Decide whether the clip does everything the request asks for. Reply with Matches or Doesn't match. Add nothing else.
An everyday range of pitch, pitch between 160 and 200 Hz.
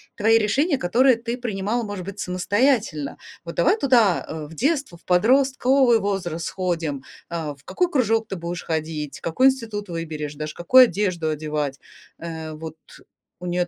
Doesn't match